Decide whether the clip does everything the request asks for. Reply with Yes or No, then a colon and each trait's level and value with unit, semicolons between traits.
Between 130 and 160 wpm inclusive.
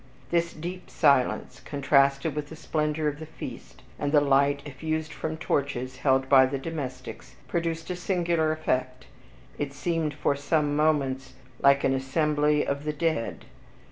Yes: average, 150 wpm